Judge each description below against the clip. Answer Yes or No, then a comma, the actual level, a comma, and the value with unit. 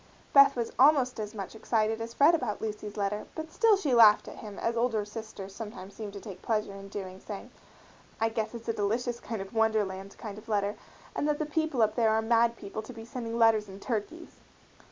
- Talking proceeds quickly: Yes, fast, 215 wpm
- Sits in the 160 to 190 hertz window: No, high, 220 Hz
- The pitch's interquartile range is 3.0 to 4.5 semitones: No, narrow, 2.4 semitones